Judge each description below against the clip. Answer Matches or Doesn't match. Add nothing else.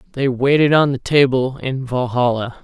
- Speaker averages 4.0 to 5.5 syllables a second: Matches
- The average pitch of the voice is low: Matches